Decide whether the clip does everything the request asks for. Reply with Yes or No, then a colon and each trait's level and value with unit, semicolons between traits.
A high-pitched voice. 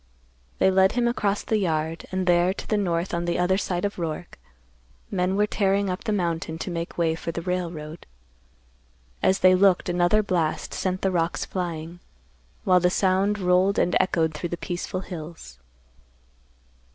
No: medium, 180 Hz